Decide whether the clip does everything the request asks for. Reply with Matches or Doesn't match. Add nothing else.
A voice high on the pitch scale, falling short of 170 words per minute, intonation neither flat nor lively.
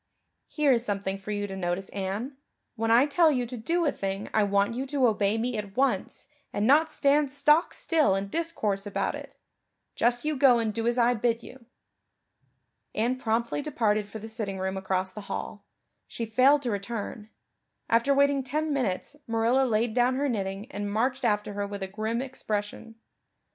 Doesn't match